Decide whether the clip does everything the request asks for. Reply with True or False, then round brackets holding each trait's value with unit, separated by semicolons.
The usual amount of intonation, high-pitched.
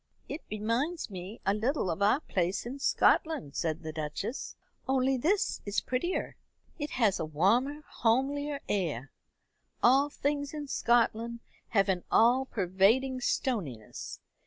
False (6.3 semitones; 235 Hz)